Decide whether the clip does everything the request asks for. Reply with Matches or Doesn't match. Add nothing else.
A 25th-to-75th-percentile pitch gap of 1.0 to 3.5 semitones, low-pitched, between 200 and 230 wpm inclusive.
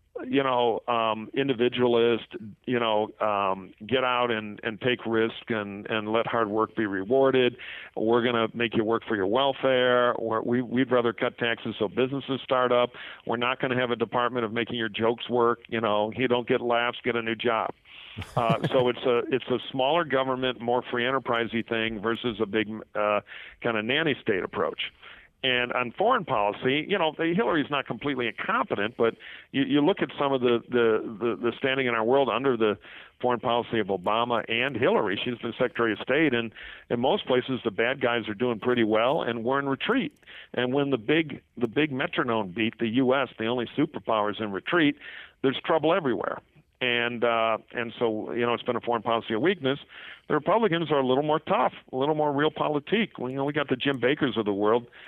Matches